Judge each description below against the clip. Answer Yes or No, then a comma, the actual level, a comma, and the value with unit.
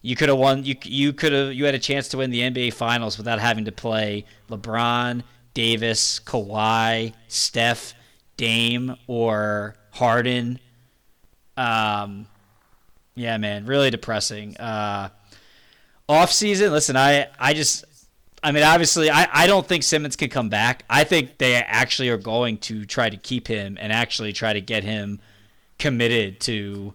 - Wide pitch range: No, average, 3.6 semitones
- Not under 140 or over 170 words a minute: Yes, average, 155 wpm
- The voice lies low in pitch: Yes, low, 115 Hz